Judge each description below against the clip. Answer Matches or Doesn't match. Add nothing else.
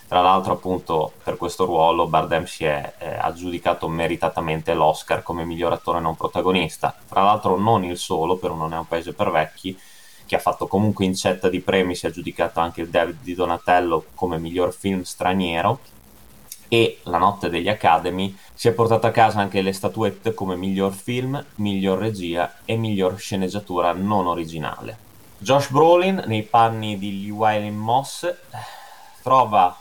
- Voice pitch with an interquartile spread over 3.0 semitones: Matches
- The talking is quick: Doesn't match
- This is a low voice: Matches